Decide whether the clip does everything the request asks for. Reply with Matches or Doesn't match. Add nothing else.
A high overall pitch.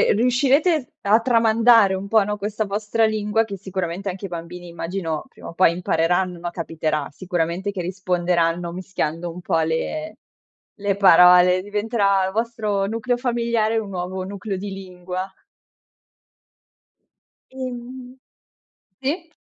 Matches